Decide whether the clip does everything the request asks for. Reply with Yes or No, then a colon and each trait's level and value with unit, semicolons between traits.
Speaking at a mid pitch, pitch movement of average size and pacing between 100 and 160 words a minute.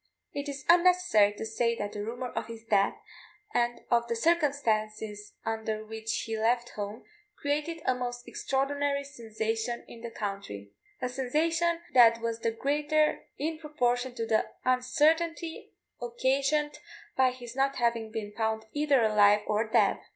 No: high, 240 Hz; average, 4.3 semitones; average, 150 wpm